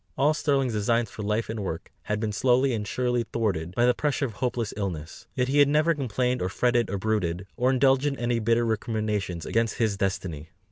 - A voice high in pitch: No, low, 115 Hz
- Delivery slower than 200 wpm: No, fast, 205 wpm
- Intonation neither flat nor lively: Yes, average, 3.8 semitones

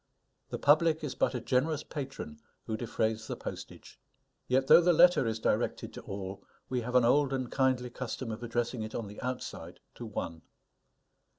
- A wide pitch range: No, average, 3.8 semitones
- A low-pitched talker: Yes, low, 125 Hz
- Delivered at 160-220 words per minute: Yes, average, 180 wpm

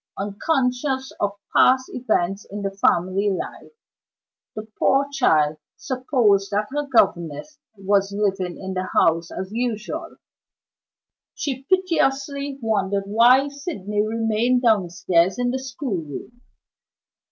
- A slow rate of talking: Yes, slow, 110 wpm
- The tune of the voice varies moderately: Yes, average, 5.0 semitones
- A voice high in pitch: Yes, high, 215 Hz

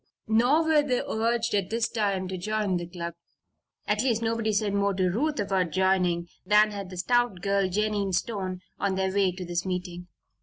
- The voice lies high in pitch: Yes, high, 200 Hz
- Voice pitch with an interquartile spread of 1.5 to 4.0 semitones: Yes, average, 3.2 semitones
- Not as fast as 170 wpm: No, average, 190 wpm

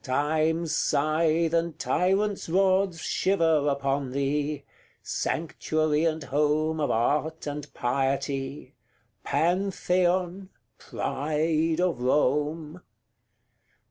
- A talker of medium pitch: Yes, medium, 155 Hz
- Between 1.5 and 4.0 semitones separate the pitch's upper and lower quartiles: Yes, average, 2.7 semitones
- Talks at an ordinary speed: No, slow, 80 wpm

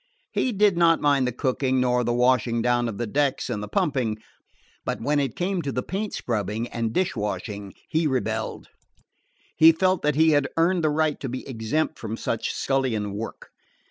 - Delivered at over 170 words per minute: Yes, average, 185 wpm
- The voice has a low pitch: Yes, low, 130 Hz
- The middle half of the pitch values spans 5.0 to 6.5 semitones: Yes, wide, 5.5 semitones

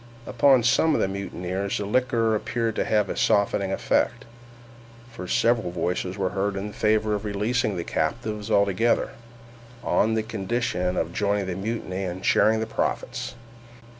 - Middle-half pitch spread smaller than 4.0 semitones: Yes, average, 2.8 semitones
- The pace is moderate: Yes, average, 150 wpm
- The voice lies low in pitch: Yes, low, 105 Hz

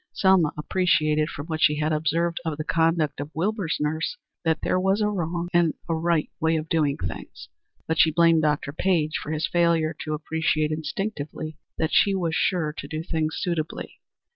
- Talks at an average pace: Yes, average, 185 wpm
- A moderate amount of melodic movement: No, narrow, 1.8 semitones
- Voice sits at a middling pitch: Yes, medium, 160 Hz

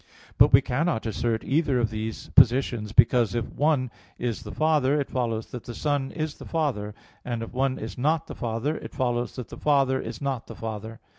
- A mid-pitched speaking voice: No, low, 125 Hz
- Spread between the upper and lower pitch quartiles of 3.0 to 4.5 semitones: Yes, average, 3.7 semitones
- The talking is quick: Yes, fast, 215 wpm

